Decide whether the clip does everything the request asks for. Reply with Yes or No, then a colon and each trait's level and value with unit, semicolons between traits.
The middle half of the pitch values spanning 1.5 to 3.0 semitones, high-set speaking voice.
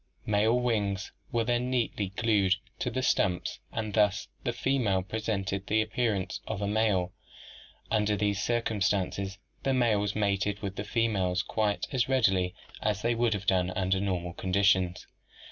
No: average, 2.7 semitones; low, 105 Hz